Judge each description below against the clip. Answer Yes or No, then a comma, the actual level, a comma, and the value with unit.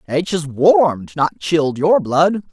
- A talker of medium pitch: Yes, medium, 155 Hz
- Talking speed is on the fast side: No, average, 165 wpm